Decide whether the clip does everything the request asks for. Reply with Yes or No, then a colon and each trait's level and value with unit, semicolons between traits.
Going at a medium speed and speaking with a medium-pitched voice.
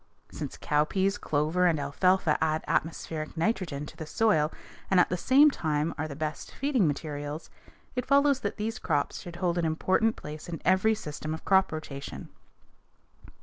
Yes: average, 165 wpm; medium, 165 Hz